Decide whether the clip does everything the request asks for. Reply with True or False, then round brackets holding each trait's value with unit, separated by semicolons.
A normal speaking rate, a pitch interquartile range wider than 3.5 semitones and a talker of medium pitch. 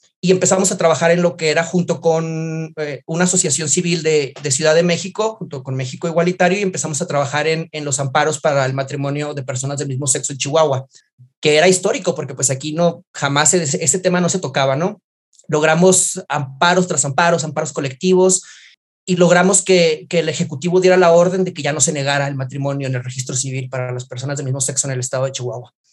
False (220 wpm; 3.9 semitones; 155 Hz)